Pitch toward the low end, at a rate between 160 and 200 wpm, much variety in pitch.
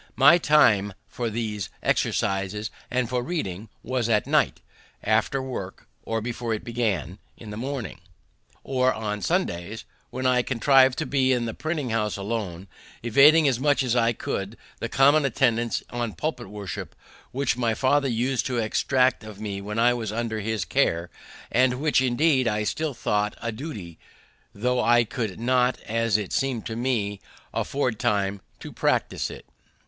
No: low, 115 Hz; average, 165 wpm; average, 3.6 semitones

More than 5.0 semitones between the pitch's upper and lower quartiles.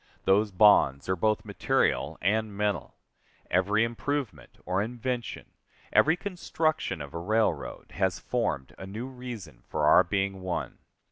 No: average, 4.2 semitones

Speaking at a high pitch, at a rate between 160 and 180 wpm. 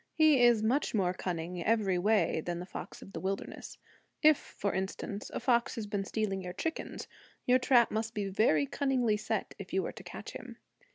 No: high, 210 Hz; average, 195 wpm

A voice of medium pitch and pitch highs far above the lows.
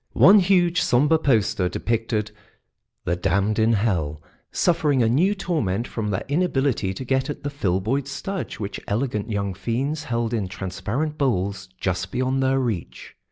No: low, 115 Hz; wide, 6.2 semitones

